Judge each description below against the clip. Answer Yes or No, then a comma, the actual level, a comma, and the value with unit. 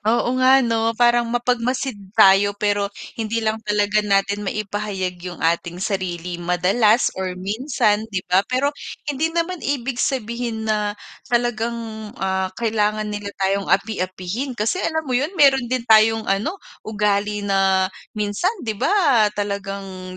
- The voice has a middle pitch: No, high, 215 Hz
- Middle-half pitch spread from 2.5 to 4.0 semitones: Yes, average, 3.5 semitones